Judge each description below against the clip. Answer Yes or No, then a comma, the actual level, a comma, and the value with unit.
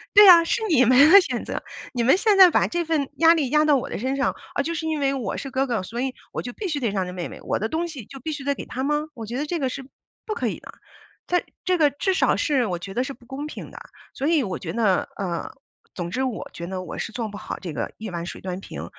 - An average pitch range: No, wide, 5.9 semitones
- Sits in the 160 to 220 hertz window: No, very high, 270 Hz